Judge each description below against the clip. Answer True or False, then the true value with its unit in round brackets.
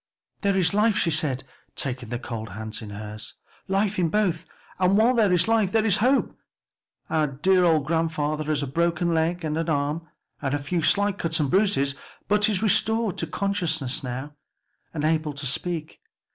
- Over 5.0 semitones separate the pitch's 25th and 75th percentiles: True (5.5 semitones)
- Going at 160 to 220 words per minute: True (180 wpm)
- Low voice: False (165 Hz)